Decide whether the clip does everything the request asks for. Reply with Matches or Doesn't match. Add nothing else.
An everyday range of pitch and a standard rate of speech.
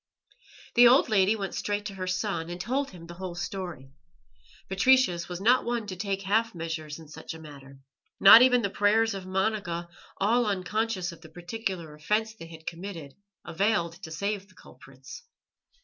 Matches